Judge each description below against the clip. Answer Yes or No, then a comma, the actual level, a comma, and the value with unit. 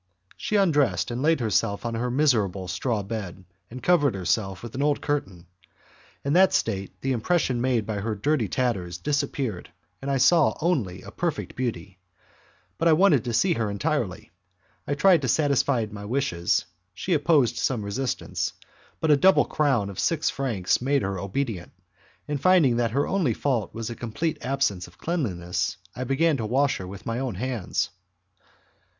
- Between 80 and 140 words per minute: No, average, 170 wpm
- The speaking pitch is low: Yes, low, 125 Hz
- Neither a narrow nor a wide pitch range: No, wide, 6.0 semitones